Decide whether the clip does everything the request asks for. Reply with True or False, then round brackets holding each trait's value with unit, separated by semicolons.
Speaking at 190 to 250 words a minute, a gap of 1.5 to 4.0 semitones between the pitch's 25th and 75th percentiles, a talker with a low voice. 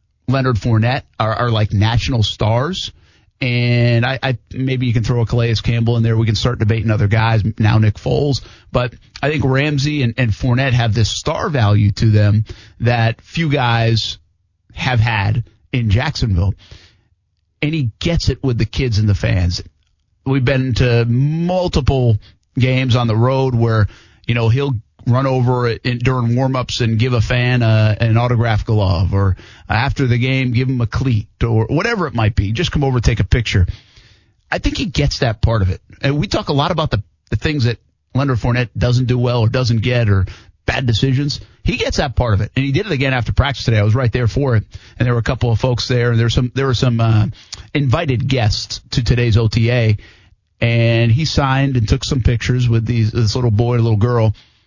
True (205 wpm; 3.0 semitones; 115 Hz)